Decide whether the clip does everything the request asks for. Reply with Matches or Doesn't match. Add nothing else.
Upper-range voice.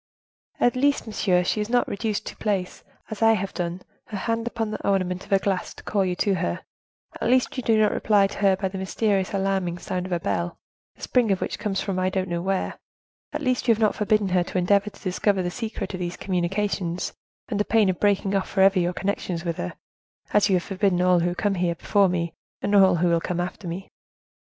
Matches